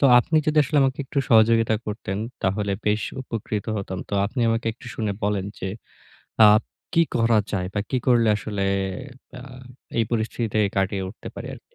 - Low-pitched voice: Yes, low, 110 Hz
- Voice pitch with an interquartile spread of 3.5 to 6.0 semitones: No, narrow, 2.6 semitones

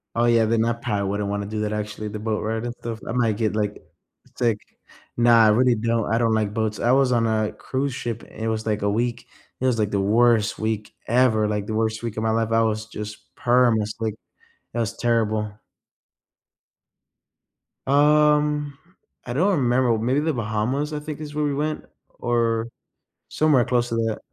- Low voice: Yes, low, 115 Hz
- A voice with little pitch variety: Yes, narrow, 2.3 semitones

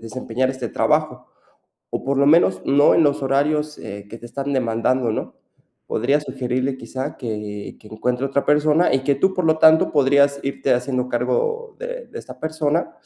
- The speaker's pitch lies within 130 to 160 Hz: Yes, low, 135 Hz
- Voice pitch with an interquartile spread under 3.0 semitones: No, average, 3.3 semitones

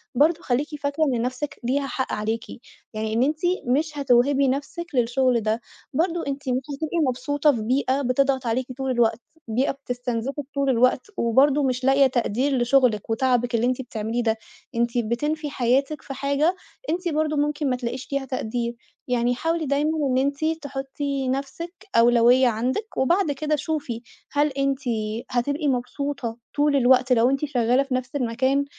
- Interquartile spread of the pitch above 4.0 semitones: No, average, 2.8 semitones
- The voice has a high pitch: Yes, very high, 265 Hz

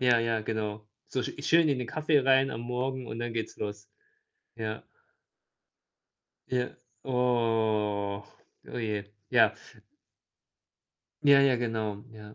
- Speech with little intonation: No, average, 3.0 semitones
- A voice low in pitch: Yes, low, 115 Hz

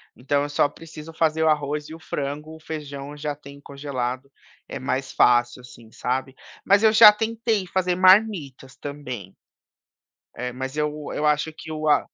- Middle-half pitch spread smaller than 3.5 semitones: Yes, average, 3.0 semitones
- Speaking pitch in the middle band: Yes, medium, 150 Hz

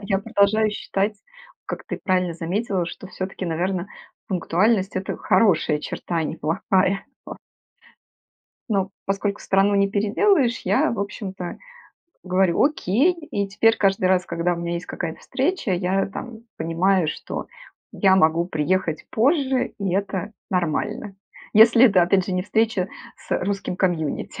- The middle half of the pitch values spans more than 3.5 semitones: No, average, 2.8 semitones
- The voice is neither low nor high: No, high, 195 Hz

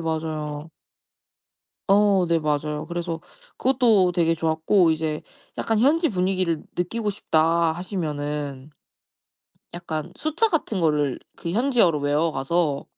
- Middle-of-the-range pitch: Yes, medium, 165 Hz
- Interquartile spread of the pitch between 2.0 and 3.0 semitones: No, average, 4.1 semitones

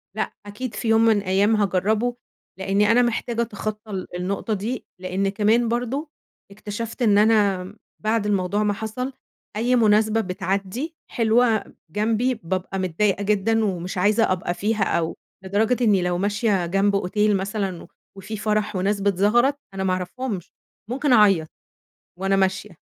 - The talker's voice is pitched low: No, high, 210 Hz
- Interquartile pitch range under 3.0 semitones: Yes, narrow, 2.6 semitones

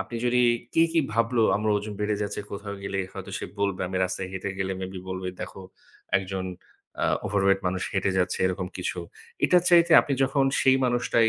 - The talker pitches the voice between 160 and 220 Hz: No, low, 100 Hz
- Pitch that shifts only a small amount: No, average, 4.1 semitones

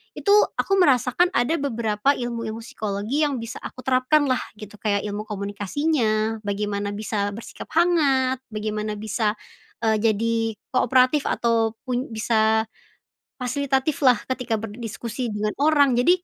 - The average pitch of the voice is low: No, high, 230 Hz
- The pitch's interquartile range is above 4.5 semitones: No, average, 3.6 semitones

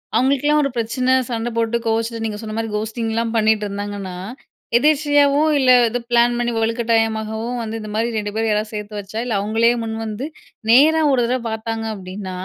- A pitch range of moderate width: No, narrow, 2.0 semitones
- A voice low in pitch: No, high, 225 Hz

